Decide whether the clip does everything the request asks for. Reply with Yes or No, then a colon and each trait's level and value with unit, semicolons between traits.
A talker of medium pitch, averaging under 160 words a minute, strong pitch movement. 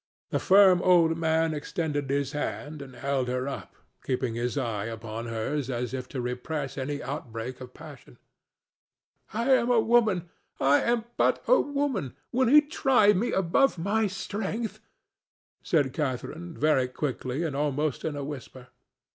Yes: medium, 150 Hz; average, 150 wpm; wide, 6.9 semitones